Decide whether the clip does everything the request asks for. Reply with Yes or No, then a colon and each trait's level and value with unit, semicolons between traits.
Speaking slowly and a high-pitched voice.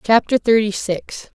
Yes: slow, 130 wpm; high, 215 Hz